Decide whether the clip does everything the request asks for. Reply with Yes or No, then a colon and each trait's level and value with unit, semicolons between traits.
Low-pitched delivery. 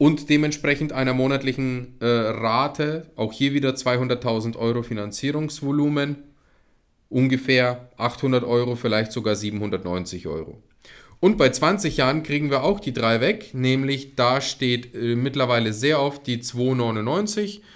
Yes: low, 130 Hz